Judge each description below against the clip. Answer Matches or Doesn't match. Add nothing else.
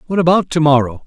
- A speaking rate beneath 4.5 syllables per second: Doesn't match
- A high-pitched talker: Doesn't match